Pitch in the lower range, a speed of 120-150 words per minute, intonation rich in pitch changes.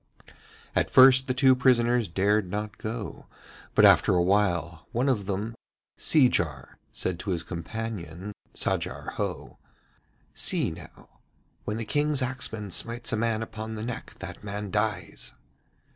No: low, 110 Hz; average, 140 wpm; average, 3.9 semitones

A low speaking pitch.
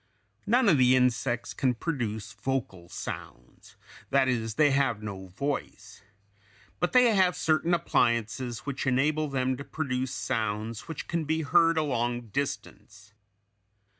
Yes: low, 130 Hz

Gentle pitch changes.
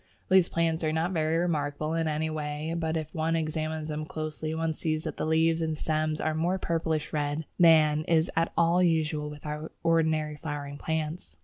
Yes: narrow, 1.1 semitones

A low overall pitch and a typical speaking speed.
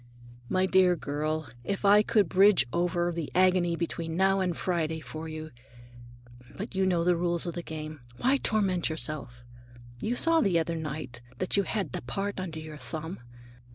No: medium, 170 Hz; average, 170 wpm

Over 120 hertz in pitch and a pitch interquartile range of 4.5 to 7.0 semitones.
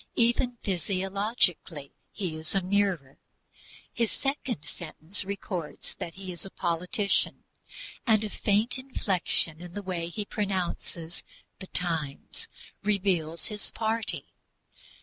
No: high, 190 Hz; average, 3.7 semitones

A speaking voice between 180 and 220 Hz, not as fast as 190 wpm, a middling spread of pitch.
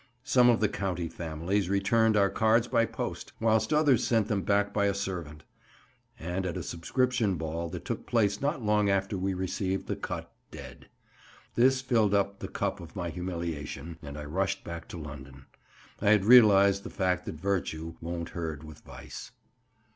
No: very low, 95 Hz; average, 175 wpm; average, 4.0 semitones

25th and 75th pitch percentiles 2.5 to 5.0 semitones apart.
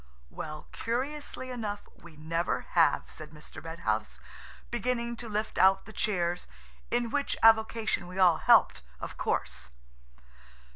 No: wide, 5.6 semitones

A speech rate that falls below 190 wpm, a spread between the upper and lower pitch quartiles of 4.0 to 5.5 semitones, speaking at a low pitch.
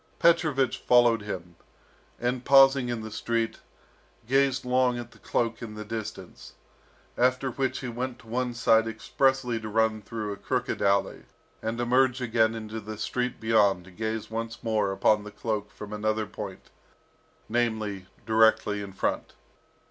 No: average, 155 wpm; narrow, 2.5 semitones; low, 115 Hz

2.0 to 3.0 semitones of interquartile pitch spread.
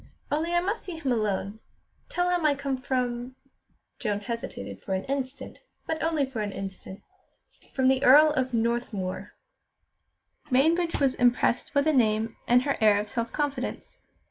No: average, 4.8 semitones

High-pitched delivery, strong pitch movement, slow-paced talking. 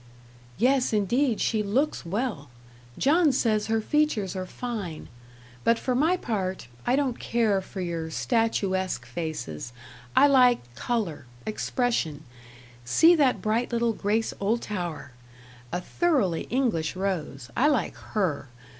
Yes: high, 215 Hz; wide, 5.9 semitones; slow, 125 wpm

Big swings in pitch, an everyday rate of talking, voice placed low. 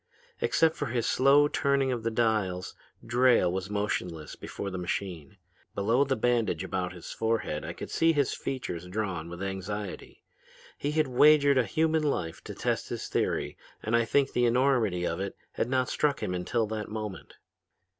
Yes: wide, 6.2 semitones; average, 175 wpm; low, 115 Hz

